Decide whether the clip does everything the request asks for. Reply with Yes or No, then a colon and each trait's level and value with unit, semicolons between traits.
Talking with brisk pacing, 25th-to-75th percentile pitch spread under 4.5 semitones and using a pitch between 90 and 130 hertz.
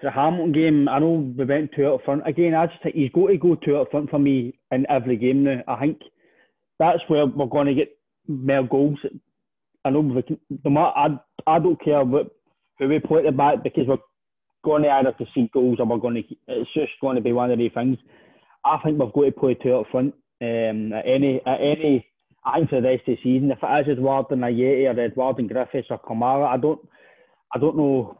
No: fast, 235 wpm; narrow, 2.6 semitones; medium, 140 Hz